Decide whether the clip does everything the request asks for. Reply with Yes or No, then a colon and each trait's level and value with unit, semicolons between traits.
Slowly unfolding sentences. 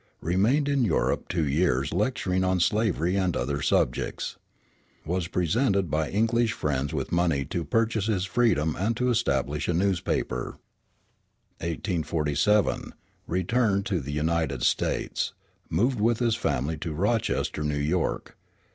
Yes: slow, 130 wpm